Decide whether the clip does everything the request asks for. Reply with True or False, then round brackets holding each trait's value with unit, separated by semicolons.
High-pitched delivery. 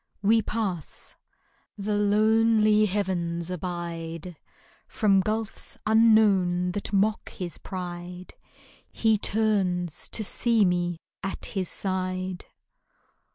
True (195 Hz)